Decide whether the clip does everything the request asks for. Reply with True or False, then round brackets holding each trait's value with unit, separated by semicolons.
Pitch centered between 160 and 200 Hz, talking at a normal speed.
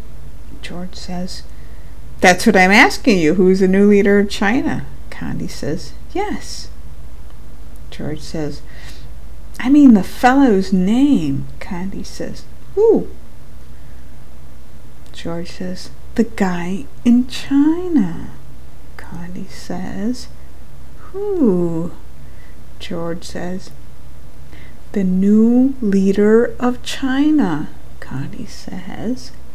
False (185 Hz; 90 wpm)